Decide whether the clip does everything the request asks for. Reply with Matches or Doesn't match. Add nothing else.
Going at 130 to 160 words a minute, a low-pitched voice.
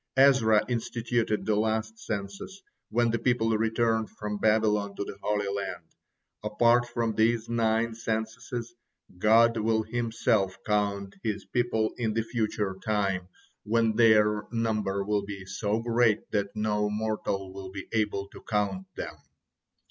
Matches